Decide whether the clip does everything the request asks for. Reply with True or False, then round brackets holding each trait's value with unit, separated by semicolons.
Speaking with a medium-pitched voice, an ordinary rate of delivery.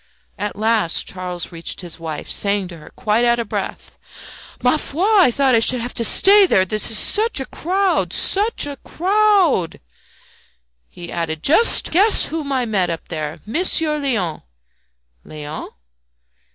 False (235 Hz; 160 wpm)